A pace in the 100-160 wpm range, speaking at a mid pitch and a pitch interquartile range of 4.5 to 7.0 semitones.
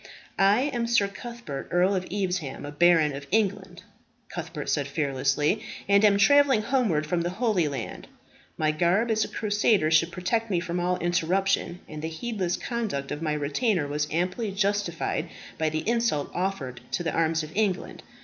No: average, 170 wpm; medium, 180 Hz; average, 4.8 semitones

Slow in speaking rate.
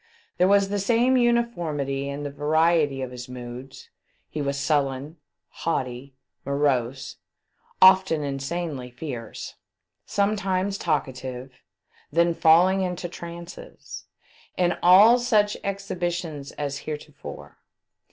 Yes: slow, 105 wpm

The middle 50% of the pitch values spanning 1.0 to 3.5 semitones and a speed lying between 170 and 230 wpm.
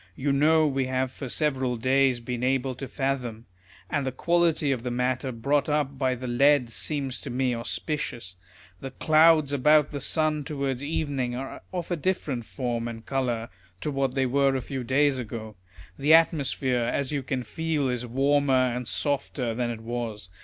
Yes: average, 2.7 semitones; average, 180 wpm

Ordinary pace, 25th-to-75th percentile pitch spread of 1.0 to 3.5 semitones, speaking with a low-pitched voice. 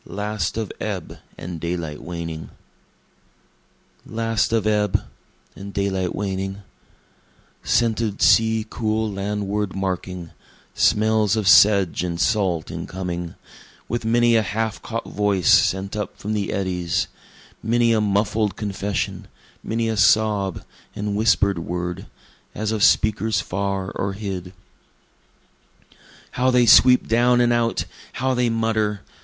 No: slow, 125 wpm; narrow, 2.6 semitones; low, 105 Hz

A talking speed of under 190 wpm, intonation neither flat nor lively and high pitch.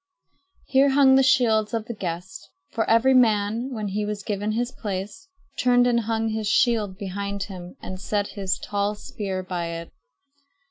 Yes: average, 170 wpm; average, 3.2 semitones; high, 210 Hz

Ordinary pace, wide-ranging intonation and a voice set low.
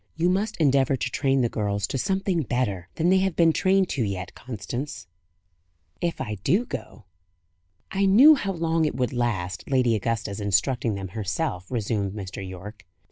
Yes: average, 170 wpm; wide, 8.4 semitones; low, 125 Hz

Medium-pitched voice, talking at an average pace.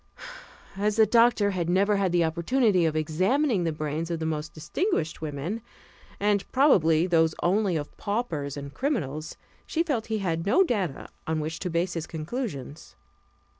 Yes: medium, 175 Hz; average, 165 wpm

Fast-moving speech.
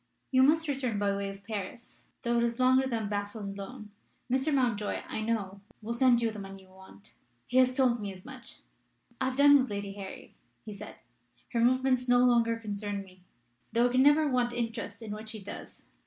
Yes: fast, 215 wpm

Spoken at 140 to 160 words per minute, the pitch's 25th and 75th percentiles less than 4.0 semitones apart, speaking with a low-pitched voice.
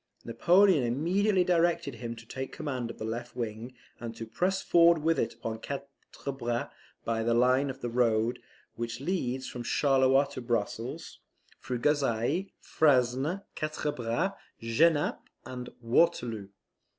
No: average, 145 wpm; average, 4.7 semitones; low, 130 Hz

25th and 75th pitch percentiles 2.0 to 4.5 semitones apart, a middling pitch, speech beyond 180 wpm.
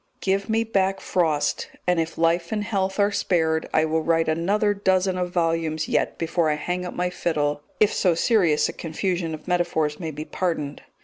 Yes: average, 3.0 semitones; medium, 170 Hz; average, 190 wpm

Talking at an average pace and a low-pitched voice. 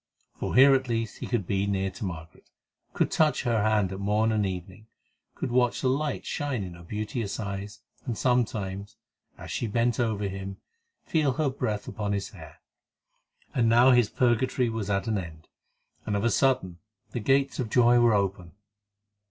Yes: average, 180 wpm; low, 110 Hz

